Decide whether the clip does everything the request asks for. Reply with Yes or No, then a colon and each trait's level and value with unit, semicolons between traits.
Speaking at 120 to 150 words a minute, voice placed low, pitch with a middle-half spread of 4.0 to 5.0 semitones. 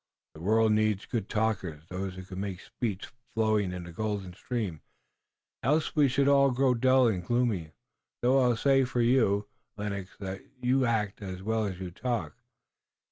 No: average, 175 wpm; low, 110 Hz; average, 4.5 semitones